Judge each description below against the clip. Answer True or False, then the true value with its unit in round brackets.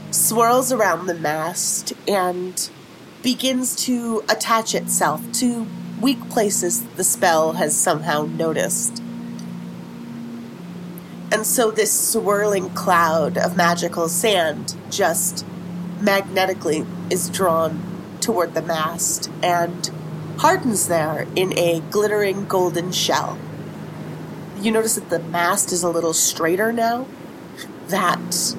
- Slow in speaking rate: True (105 wpm)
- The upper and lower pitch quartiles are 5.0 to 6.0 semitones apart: False (3.8 semitones)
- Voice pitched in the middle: True (180 Hz)